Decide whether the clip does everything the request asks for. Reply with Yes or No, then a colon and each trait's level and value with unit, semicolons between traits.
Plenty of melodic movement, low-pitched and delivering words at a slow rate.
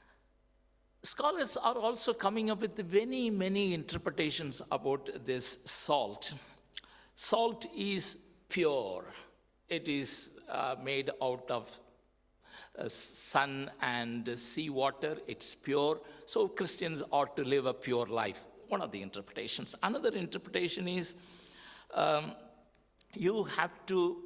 No: wide, 7.4 semitones; medium, 165 Hz; slow, 115 wpm